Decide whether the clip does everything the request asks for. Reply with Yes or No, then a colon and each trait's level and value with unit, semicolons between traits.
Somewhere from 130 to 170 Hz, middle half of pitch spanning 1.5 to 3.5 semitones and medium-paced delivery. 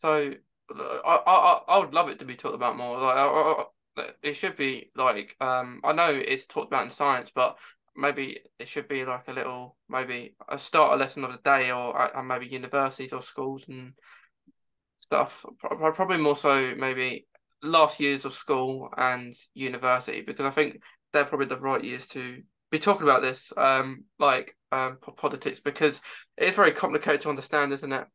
Yes: low, 135 Hz; narrow, 2.4 semitones; average, 185 wpm